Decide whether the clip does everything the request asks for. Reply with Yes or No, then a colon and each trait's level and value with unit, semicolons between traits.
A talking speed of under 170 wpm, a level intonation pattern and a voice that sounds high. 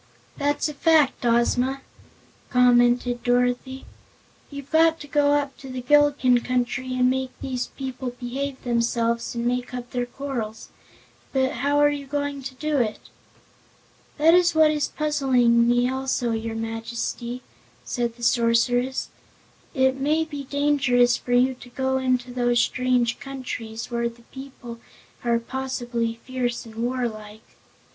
Yes: average, 140 wpm; narrow, 2.3 semitones; very high, 250 Hz